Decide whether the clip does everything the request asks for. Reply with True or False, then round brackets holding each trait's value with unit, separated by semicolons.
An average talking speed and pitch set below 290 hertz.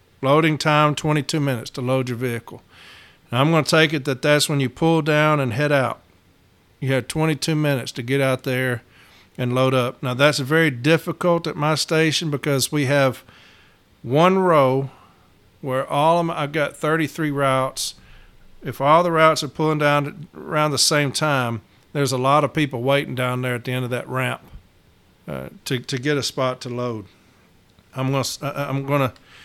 True (190 wpm; 135 Hz)